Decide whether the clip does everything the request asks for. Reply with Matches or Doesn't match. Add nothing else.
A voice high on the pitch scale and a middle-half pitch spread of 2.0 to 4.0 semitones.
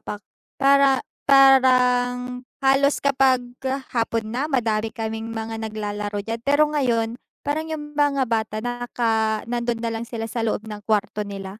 Matches